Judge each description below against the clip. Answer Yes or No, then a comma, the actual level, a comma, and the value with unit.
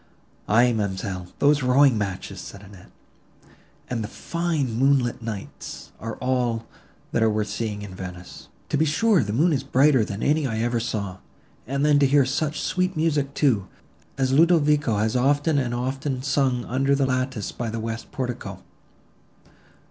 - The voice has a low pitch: Yes, low, 125 Hz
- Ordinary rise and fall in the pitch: Yes, average, 4.4 semitones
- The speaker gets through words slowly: No, average, 165 wpm